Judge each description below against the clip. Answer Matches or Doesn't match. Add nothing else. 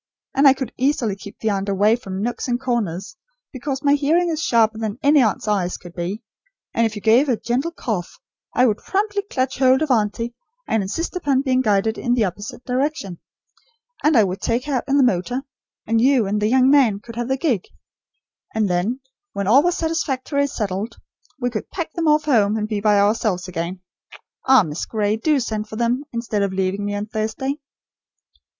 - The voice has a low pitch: Doesn't match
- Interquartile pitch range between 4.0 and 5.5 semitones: Matches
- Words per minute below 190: Doesn't match